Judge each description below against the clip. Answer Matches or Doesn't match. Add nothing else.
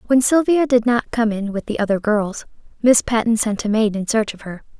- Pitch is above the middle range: Matches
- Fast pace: Matches